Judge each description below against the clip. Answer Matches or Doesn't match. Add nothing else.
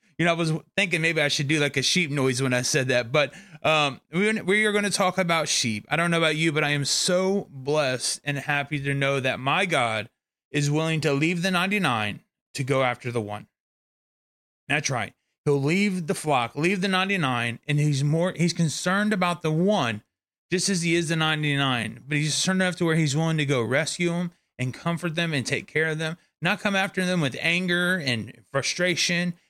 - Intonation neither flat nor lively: Matches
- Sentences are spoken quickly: Matches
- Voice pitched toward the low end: Doesn't match